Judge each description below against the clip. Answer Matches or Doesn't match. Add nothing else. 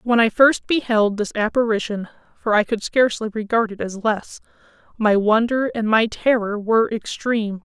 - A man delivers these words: Doesn't match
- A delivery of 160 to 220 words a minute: Doesn't match